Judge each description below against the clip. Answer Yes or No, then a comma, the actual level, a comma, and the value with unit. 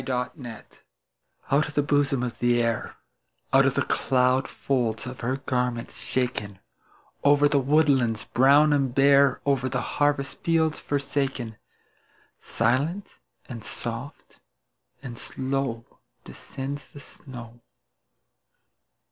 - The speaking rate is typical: No, slow, 115 wpm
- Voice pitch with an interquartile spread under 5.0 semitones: Yes, average, 2.8 semitones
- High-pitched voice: No, low, 135 Hz